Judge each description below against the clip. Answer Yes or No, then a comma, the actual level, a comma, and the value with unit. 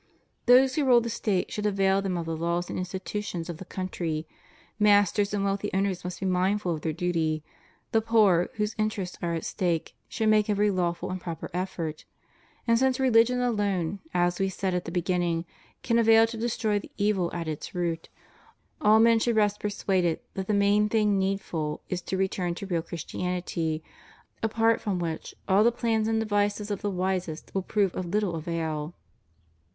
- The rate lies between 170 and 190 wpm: Yes, average, 185 wpm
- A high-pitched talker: Yes, high, 195 Hz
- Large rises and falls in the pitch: No, average, 3.4 semitones